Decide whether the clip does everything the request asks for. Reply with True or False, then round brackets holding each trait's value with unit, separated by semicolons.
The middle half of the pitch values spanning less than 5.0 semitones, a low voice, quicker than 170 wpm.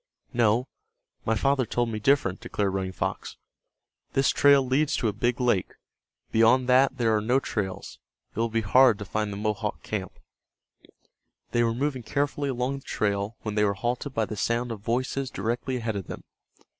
True (3.4 semitones; 115 Hz; 180 wpm)